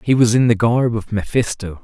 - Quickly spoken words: Yes, fast, 230 wpm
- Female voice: No, male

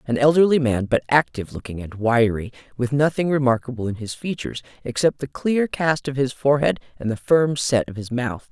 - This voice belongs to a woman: Yes, female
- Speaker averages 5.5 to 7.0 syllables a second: Yes, 5.6 syllables/s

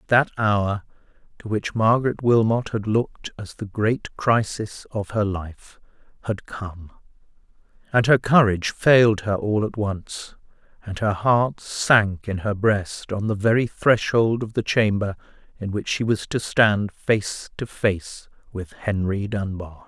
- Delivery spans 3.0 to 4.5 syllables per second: Yes, 3.9 syllables/s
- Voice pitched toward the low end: Yes, low, 105 Hz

